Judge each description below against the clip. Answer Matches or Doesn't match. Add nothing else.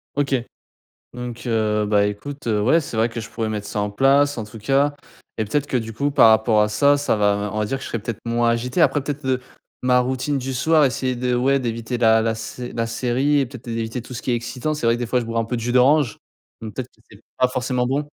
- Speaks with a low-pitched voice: Matches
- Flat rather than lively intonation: Doesn't match